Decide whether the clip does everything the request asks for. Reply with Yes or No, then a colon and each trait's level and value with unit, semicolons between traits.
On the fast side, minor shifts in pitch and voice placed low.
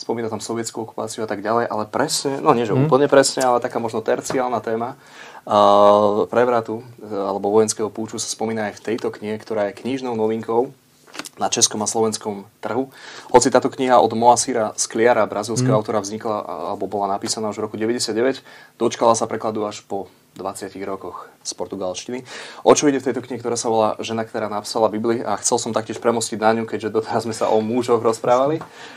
Yes: fast, 185 wpm; narrow, 2.1 semitones; low, 115 Hz